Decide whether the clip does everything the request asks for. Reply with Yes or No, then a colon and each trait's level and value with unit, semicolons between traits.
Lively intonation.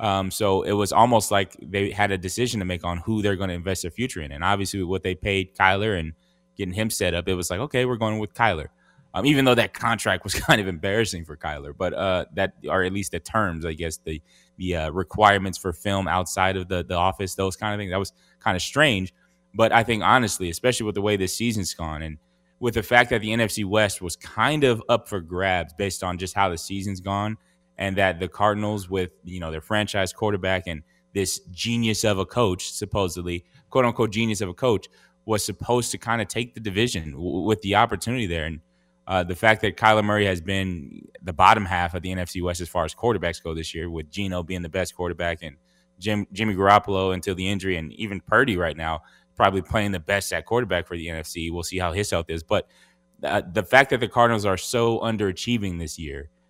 No: average, 3.4 semitones